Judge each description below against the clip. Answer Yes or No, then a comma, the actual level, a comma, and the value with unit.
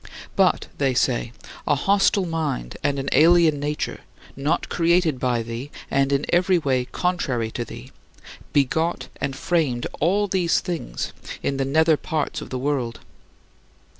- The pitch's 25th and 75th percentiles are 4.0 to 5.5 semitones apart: Yes, average, 4.6 semitones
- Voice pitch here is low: No, medium, 145 Hz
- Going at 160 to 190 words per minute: No, average, 145 wpm